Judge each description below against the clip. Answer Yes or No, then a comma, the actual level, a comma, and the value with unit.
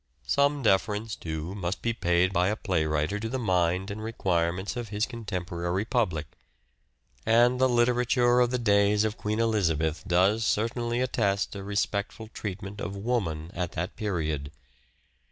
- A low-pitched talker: Yes, low, 100 Hz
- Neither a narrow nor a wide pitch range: Yes, average, 4.5 semitones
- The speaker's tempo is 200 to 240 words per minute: No, average, 155 wpm